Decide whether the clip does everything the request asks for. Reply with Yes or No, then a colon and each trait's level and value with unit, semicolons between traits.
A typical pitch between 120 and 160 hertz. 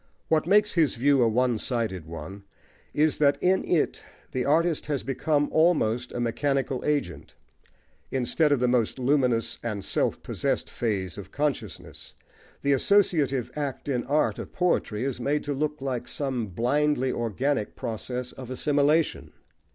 Yes: low, 135 Hz